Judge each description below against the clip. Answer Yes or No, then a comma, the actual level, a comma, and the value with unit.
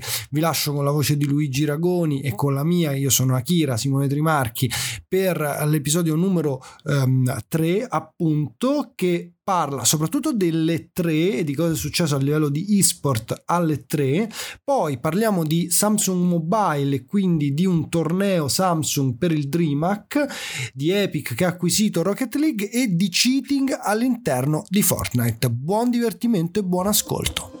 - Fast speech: No, average, 150 wpm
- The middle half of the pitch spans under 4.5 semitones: No, average, 5.0 semitones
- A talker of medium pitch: Yes, medium, 165 Hz